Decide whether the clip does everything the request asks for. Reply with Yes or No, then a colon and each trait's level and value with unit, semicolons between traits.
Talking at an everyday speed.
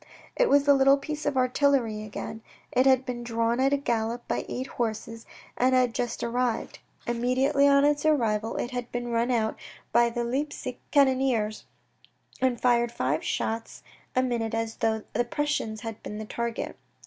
Yes: average, 170 wpm